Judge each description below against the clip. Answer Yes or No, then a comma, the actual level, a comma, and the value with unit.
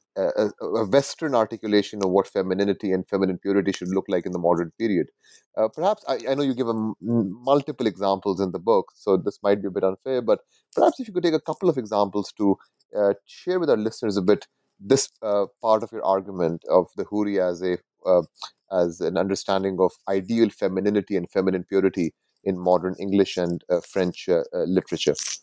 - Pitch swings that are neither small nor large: Yes, average, 3.2 semitones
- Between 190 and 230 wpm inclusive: Yes, fast, 205 wpm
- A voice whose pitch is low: Yes, low, 100 Hz